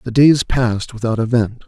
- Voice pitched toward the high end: No, low, 120 Hz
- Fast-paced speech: No, average, 180 wpm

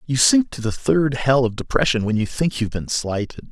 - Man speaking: Yes, male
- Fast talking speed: Yes, fast, 240 wpm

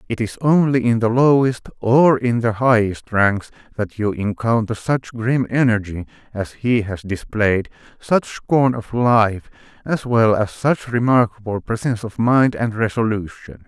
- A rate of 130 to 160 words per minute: Yes, average, 155 wpm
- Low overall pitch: Yes, low, 115 Hz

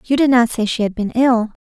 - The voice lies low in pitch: No, high, 235 Hz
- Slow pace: No, fast, 295 wpm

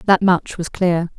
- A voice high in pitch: No, medium, 180 Hz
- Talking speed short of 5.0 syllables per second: Yes, 4.0 syllables/s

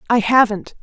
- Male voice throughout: No, female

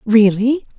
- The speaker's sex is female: Yes, female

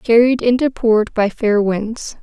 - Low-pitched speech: No, high, 225 Hz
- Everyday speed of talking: Yes, average, 160 wpm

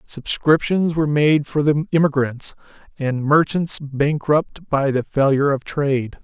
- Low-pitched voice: No, medium, 145 Hz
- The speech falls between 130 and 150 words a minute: Yes, slow, 135 wpm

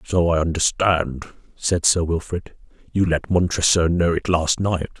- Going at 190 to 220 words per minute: No, average, 155 wpm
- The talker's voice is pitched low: Yes, very low, 85 Hz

